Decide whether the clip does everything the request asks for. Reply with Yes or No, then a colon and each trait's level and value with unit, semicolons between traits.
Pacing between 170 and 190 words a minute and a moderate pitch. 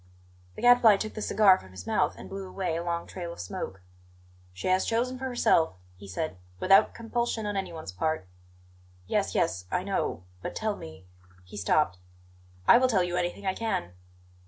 Yes: average, 185 wpm; medium, 180 Hz